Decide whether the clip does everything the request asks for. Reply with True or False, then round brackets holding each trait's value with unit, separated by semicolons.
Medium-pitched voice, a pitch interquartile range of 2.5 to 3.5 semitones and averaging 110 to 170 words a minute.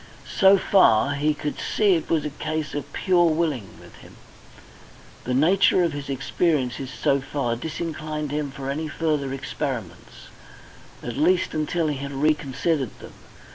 True (150 Hz; 2.9 semitones; 150 wpm)